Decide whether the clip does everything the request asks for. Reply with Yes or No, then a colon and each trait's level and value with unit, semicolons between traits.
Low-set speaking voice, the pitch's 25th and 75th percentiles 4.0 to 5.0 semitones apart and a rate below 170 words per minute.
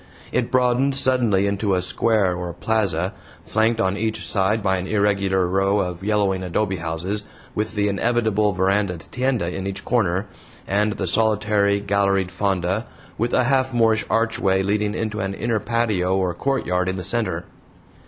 No: low, 100 Hz; average, 2.9 semitones; average, 160 wpm